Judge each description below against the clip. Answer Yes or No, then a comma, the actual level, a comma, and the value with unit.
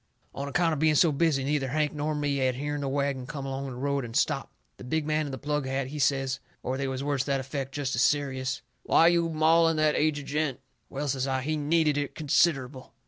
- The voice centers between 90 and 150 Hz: Yes, medium, 140 Hz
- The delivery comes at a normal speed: No, fast, 245 wpm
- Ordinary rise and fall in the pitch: No, narrow, 2.2 semitones